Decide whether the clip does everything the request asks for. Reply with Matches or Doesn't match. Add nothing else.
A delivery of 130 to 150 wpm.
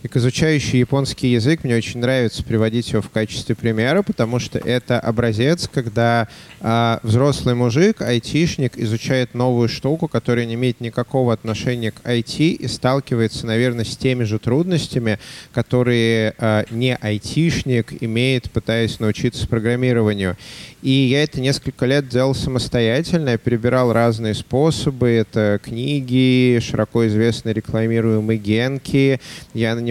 Matches